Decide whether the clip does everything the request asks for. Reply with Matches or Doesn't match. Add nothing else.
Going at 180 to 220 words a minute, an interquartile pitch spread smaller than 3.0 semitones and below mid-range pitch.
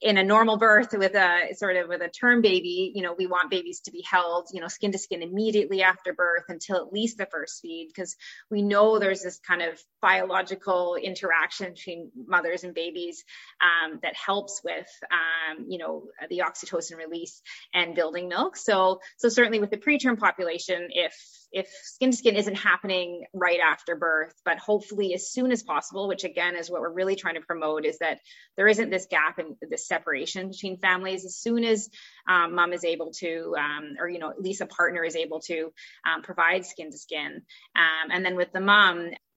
Doesn't match